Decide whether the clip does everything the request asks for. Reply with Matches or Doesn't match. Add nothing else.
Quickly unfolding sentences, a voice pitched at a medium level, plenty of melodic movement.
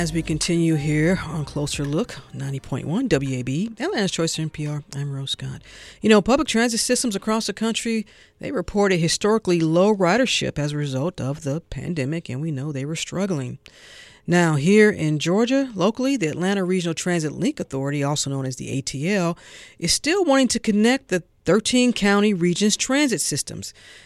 Doesn't match